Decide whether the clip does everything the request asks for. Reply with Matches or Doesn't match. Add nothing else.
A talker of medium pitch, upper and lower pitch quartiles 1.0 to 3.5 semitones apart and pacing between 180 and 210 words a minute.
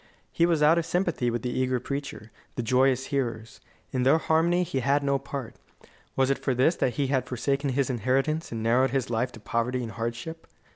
Doesn't match